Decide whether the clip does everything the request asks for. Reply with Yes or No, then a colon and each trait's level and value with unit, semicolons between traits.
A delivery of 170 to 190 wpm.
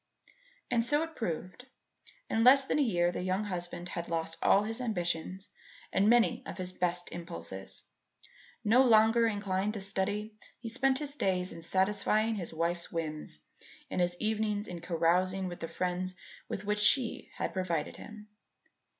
No: average, 160 wpm